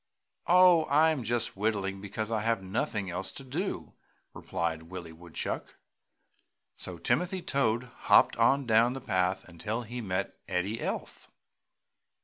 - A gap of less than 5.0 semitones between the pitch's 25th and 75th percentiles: No, wide, 5.4 semitones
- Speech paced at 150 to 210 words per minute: No, slow, 135 wpm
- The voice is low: Yes, low, 110 Hz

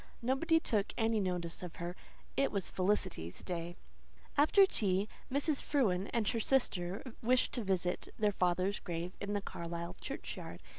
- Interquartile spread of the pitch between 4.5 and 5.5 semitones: Yes, average, 5.2 semitones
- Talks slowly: No, average, 150 wpm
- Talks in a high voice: Yes, high, 200 Hz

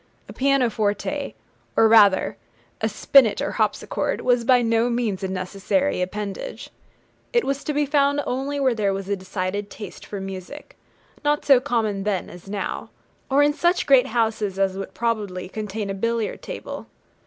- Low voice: No, high, 225 Hz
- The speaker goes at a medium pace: Yes, average, 165 wpm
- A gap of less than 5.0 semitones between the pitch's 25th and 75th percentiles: No, wide, 5.6 semitones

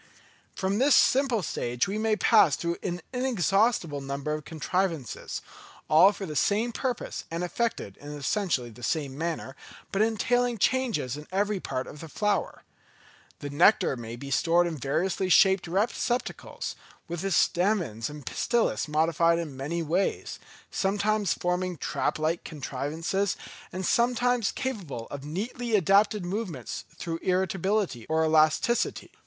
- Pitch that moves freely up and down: Yes, wide, 5.7 semitones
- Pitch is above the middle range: No, medium, 175 Hz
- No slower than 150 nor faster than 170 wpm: No, average, 140 wpm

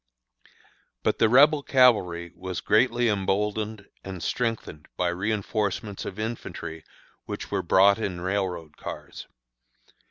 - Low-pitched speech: Yes, low, 100 Hz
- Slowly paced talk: Yes, slow, 115 wpm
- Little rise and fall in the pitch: No, average, 3.5 semitones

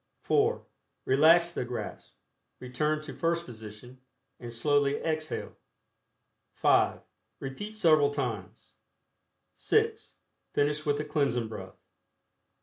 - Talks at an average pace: No, slow, 100 wpm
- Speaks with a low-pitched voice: No, medium, 145 Hz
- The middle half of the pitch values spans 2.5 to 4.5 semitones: Yes, average, 4.0 semitones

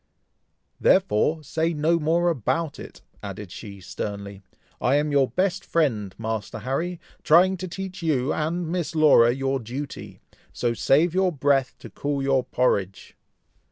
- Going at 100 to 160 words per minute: Yes, average, 145 wpm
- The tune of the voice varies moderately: No, wide, 5.9 semitones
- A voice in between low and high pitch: Yes, medium, 145 Hz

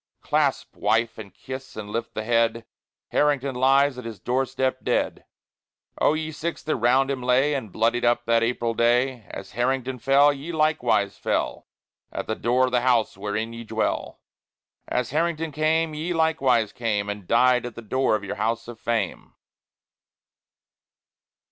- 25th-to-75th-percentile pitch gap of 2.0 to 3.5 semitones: Yes, average, 2.9 semitones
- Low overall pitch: Yes, low, 125 Hz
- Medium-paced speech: Yes, average, 165 wpm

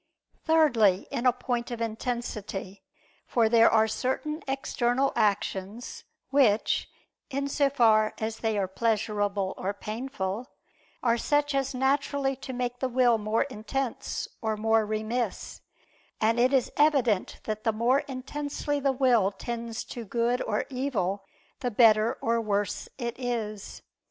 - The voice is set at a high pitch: Yes, high, 235 Hz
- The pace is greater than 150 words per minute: No, slow, 135 wpm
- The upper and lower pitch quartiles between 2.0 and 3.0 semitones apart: No, average, 3.4 semitones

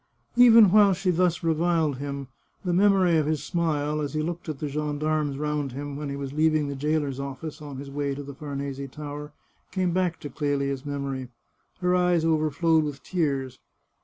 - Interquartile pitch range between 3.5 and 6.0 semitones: No, average, 3.0 semitones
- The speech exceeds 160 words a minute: Yes, average, 185 wpm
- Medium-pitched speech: Yes, medium, 150 Hz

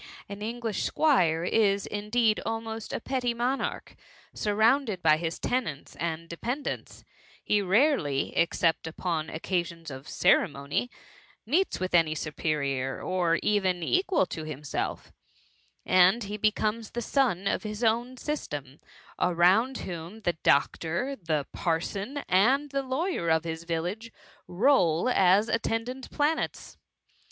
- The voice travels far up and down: Yes, wide, 6.4 semitones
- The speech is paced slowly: Yes, slow, 125 wpm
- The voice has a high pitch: Yes, high, 200 Hz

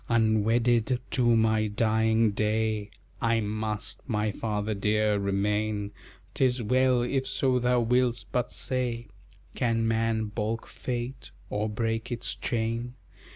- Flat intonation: Yes, narrow, 2.1 semitones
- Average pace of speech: No, slow, 120 wpm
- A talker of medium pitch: No, low, 115 Hz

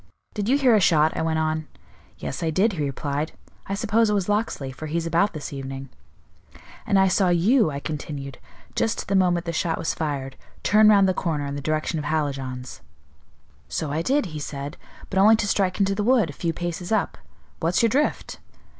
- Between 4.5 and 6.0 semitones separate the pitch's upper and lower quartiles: Yes, average, 5.3 semitones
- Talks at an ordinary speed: No, fast, 210 wpm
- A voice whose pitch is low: No, medium, 170 Hz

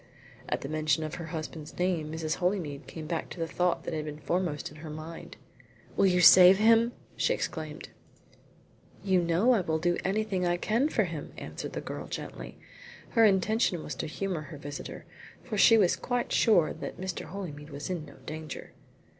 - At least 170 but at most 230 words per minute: Yes, average, 190 wpm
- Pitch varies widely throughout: No, average, 3.6 semitones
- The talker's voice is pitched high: No, medium, 175 Hz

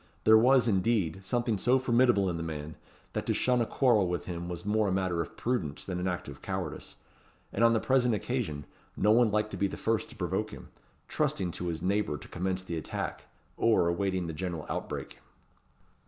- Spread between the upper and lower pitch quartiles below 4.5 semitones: No, average, 5.0 semitones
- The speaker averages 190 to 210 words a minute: Yes, average, 200 wpm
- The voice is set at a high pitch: No, very low, 95 Hz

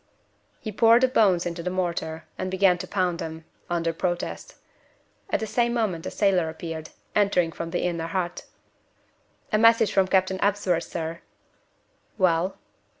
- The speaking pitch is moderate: Yes, medium, 180 Hz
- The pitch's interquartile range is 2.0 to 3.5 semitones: Yes, average, 3.1 semitones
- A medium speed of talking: Yes, average, 150 wpm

